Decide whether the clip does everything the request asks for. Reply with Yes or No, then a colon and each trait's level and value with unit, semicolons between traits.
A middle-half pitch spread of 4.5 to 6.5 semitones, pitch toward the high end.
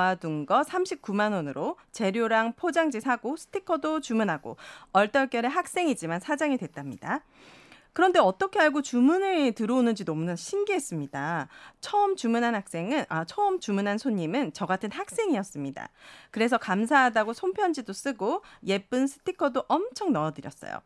No: wide, 8.1 semitones; high, 235 Hz